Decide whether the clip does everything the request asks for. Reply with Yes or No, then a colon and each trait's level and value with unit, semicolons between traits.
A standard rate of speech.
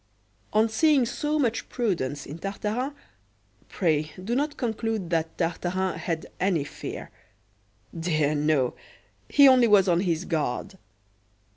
No: slow, 125 wpm